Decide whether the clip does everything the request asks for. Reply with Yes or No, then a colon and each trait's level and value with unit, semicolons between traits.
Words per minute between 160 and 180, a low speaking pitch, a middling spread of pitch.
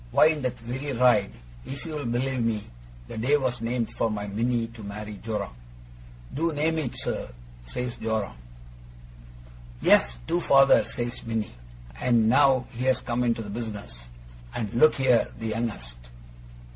No: average, 150 wpm; low, 120 Hz; average, 3.3 semitones